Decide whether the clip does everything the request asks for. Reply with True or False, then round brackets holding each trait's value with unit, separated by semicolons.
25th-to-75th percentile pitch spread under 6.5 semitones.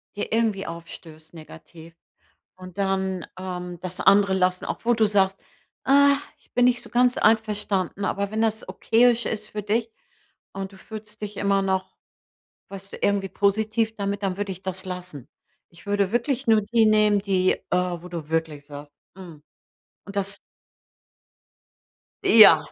True (2.9 semitones)